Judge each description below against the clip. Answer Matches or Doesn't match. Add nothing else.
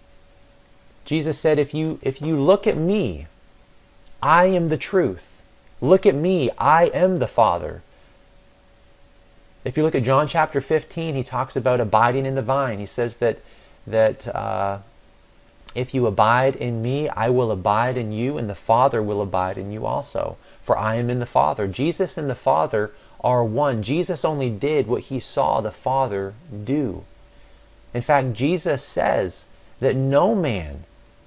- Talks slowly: Doesn't match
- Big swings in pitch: Matches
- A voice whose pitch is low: Matches